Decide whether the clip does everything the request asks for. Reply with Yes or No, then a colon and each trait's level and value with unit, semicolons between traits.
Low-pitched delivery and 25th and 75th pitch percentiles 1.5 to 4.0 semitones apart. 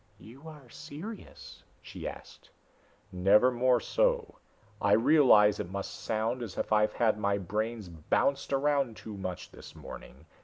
No: low, 115 Hz; wide, 5.5 semitones